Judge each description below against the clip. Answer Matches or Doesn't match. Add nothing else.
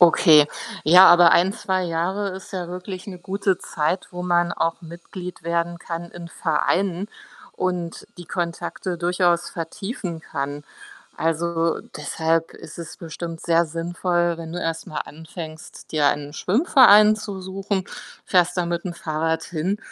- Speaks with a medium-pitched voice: Matches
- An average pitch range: Doesn't match